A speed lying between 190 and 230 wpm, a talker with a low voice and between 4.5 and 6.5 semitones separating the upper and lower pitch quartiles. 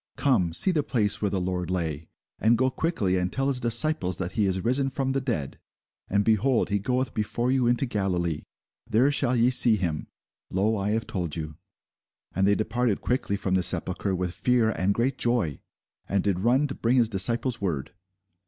Yes: average, 195 wpm; low, 110 Hz; average, 5.1 semitones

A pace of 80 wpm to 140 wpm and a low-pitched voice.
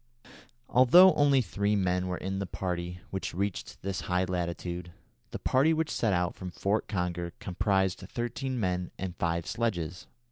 No: average, 155 wpm; very low, 95 Hz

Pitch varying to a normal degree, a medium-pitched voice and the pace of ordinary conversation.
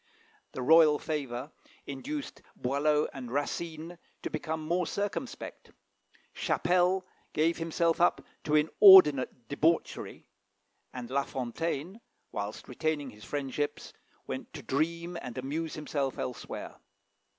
No: average, 3.7 semitones; medium, 155 Hz; slow, 110 wpm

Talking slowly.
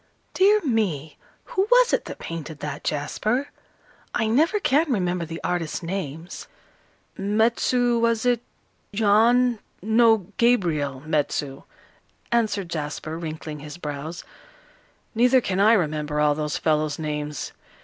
Yes: slow, 120 wpm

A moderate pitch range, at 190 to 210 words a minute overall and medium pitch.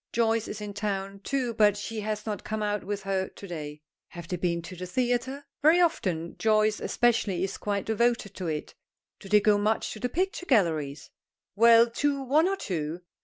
No: average, 3.9 semitones; average, 195 wpm; high, 210 Hz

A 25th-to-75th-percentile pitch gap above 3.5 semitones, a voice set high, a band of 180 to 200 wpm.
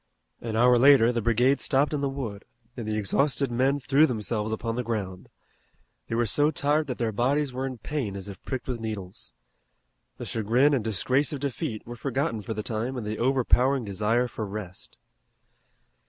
No: average, 3.9 semitones; low, 120 Hz; average, 185 wpm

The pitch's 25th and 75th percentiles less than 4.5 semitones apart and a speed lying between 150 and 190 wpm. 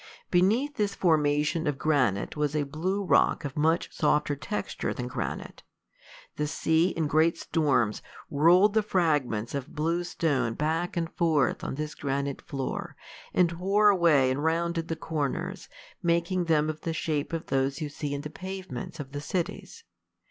Yes: average, 3.2 semitones; average, 165 wpm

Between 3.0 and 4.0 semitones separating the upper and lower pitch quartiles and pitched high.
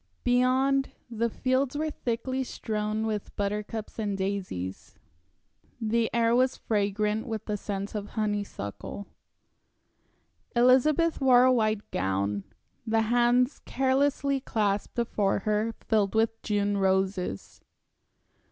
Yes: average, 3.6 semitones; high, 220 Hz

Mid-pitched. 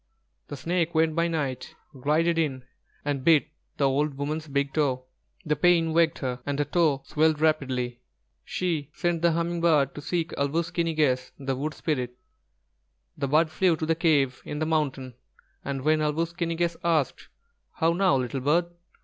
Yes: medium, 155 Hz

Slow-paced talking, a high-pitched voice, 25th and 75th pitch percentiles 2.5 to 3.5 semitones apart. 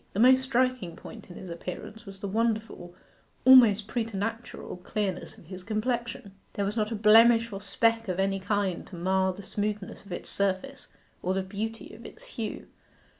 No: average, 175 wpm; high, 210 Hz; average, 3.1 semitones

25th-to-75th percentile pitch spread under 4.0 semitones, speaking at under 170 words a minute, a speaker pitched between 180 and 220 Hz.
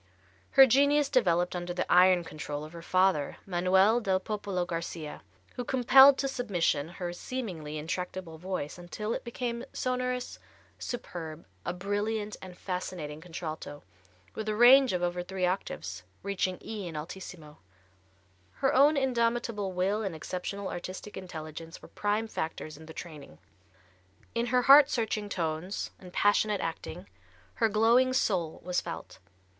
No: average, 5.1 semitones; average, 140 wpm; medium, 185 Hz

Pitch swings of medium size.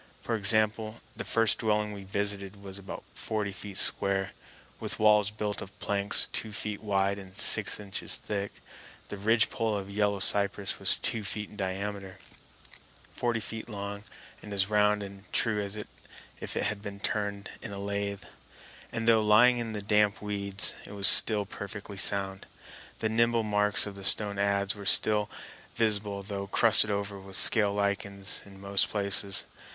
No: narrow, 1.2 semitones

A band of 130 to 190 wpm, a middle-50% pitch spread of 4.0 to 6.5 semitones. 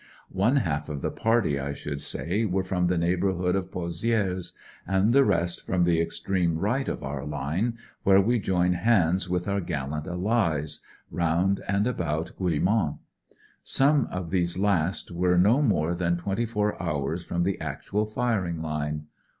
No: average, 160 wpm; average, 3.4 semitones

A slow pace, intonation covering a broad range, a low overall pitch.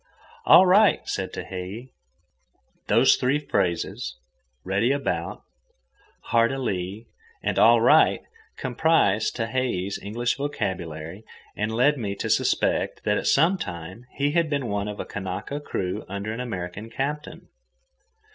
Yes: slow, 130 wpm; wide, 6.4 semitones; low, 115 Hz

